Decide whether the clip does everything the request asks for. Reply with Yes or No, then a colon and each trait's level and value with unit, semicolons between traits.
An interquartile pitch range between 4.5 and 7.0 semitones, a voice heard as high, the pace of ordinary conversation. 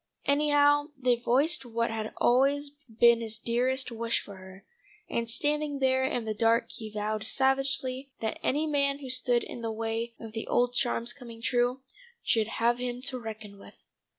No: average, 2.9 semitones; high, 240 Hz; average, 175 wpm